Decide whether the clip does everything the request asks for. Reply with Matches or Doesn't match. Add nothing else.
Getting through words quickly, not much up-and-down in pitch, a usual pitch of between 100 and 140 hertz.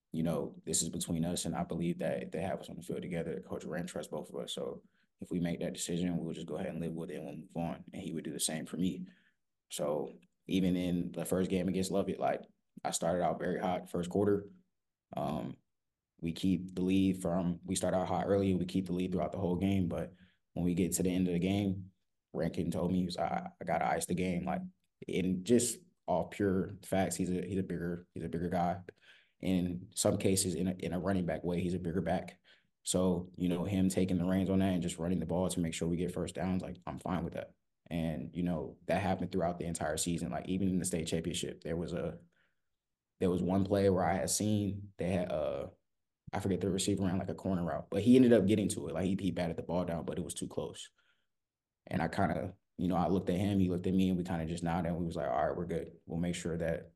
Doesn't match